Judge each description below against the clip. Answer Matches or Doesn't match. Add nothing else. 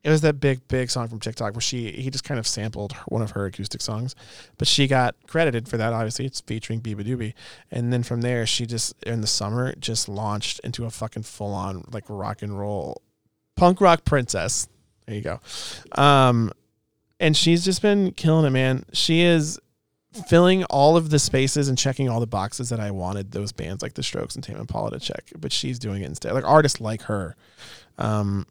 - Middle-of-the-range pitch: Doesn't match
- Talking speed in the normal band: Doesn't match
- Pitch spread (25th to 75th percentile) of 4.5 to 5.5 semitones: Matches